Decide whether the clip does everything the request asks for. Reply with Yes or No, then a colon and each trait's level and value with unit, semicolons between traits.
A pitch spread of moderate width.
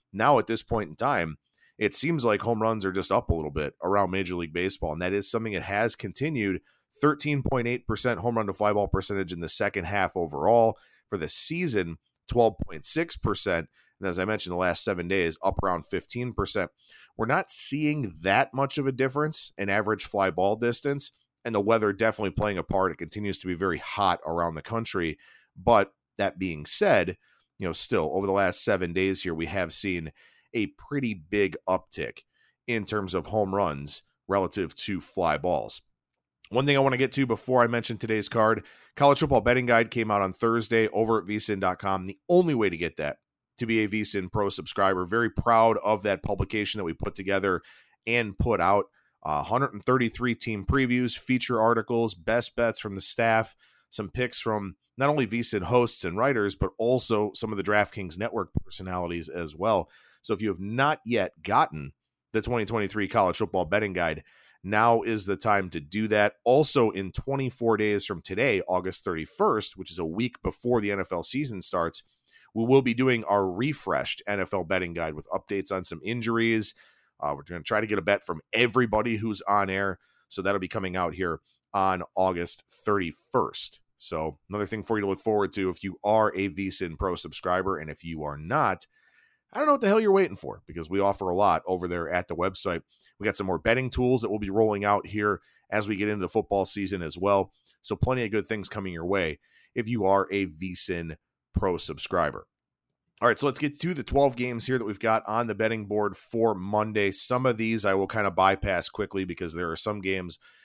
Yes: average, 3.6 semitones